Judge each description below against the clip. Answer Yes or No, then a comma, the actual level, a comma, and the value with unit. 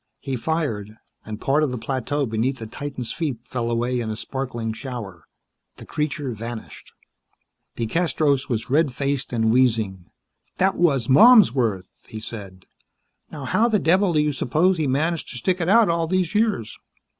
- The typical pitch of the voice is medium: No, low, 130 Hz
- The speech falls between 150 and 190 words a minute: Yes, average, 165 wpm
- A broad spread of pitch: Yes, wide, 5.8 semitones